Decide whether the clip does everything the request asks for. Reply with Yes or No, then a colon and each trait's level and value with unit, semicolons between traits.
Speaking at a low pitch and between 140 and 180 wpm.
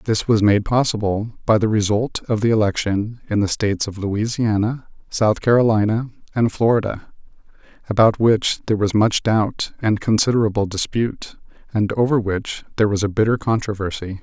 Yes: low, 110 Hz; average, 150 wpm